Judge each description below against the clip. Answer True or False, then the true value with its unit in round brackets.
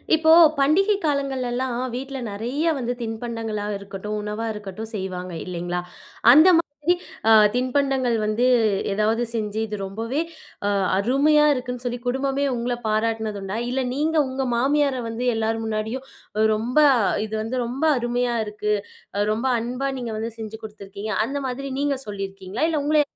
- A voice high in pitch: True (235 Hz)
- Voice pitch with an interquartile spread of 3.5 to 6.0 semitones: True (4.0 semitones)